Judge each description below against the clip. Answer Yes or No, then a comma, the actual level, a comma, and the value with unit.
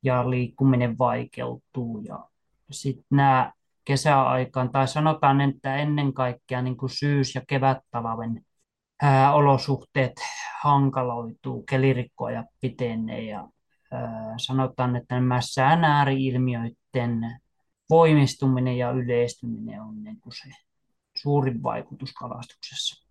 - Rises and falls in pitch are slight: Yes, narrow, 2.1 semitones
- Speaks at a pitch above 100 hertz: Yes, low, 130 Hz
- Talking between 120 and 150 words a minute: No, slow, 95 wpm